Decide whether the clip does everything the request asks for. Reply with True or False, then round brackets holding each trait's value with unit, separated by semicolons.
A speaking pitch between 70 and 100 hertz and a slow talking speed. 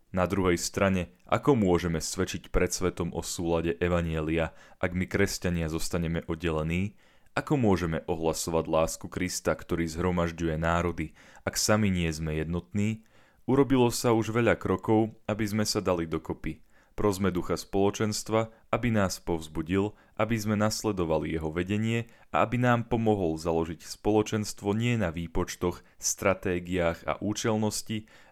False (90 Hz; 130 wpm)